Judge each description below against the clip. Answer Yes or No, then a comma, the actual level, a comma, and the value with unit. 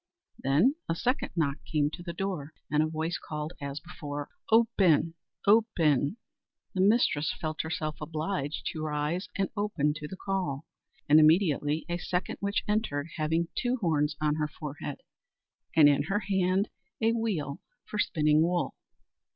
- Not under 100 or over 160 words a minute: Yes, average, 150 wpm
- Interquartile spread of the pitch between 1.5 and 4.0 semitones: No, average, 4.4 semitones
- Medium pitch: Yes, medium, 160 Hz